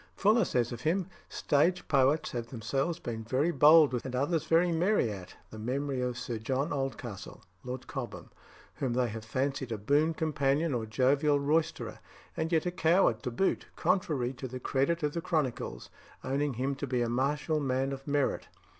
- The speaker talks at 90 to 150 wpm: No, average, 180 wpm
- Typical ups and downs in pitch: Yes, average, 4.1 semitones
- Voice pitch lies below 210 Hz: Yes, low, 135 Hz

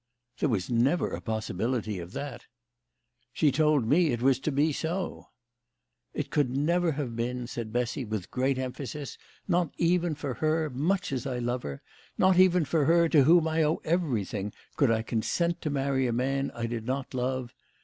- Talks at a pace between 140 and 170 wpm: No, average, 195 wpm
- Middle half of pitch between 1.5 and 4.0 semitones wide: No, average, 4.6 semitones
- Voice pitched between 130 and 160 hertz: Yes, low, 135 Hz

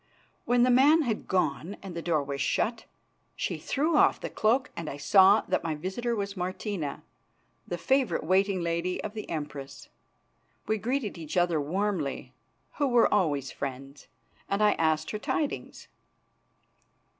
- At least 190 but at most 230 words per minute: No, average, 155 wpm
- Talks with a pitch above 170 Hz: Yes, high, 190 Hz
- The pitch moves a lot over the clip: Yes, wide, 5.8 semitones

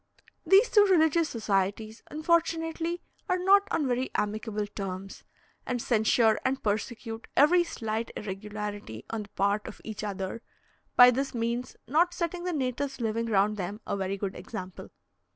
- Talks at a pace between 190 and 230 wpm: No, average, 150 wpm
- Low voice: No, high, 230 Hz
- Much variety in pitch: Yes, wide, 7.1 semitones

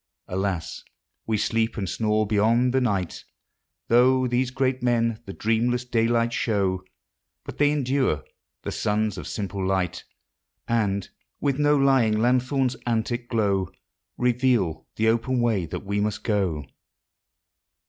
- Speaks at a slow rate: Yes, slow, 130 wpm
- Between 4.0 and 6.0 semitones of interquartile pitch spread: No, average, 3.6 semitones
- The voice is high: No, low, 115 Hz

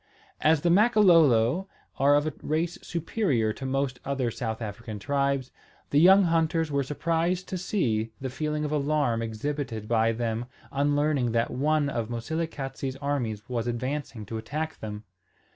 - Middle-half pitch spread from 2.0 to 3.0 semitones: No, average, 4.9 semitones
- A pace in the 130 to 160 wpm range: Yes, average, 155 wpm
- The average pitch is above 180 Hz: No, medium, 140 Hz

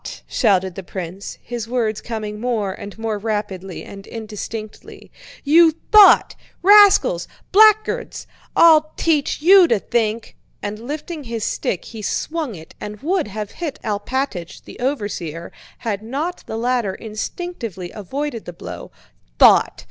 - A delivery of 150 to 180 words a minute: No, slow, 135 wpm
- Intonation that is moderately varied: No, wide, 6.5 semitones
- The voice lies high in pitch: Yes, high, 225 Hz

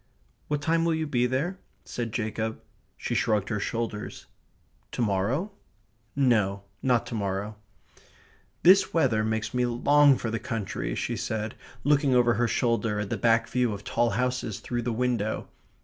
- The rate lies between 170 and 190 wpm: No, average, 160 wpm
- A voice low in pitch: Yes, low, 120 Hz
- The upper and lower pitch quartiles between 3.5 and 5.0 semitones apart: No, average, 3.0 semitones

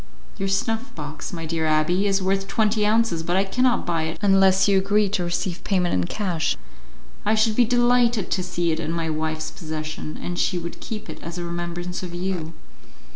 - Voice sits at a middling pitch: Yes, medium, 180 Hz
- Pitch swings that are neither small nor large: Yes, average, 3.7 semitones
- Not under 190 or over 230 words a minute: Yes, average, 200 wpm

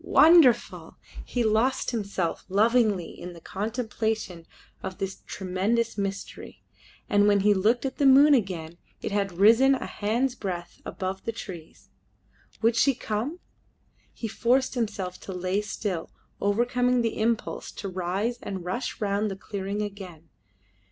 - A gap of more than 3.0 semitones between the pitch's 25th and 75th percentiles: Yes, average, 3.8 semitones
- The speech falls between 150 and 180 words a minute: No, average, 140 wpm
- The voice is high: Yes, high, 210 Hz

